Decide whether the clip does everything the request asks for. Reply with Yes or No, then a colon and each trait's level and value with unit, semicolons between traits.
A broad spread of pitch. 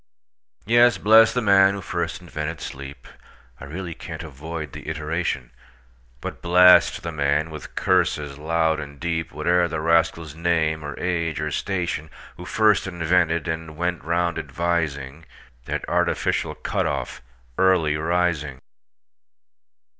No: average, 2.7 semitones